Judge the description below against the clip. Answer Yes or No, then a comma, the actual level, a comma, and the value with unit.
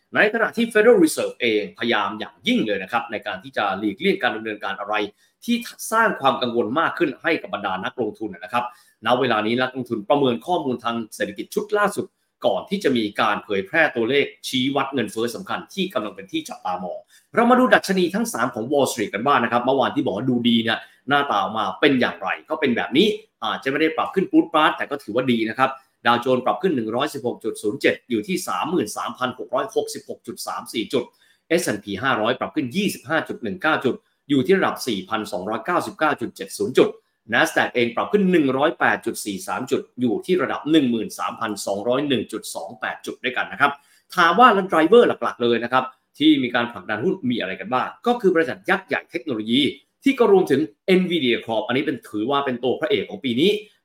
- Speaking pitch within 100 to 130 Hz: No, medium, 140 Hz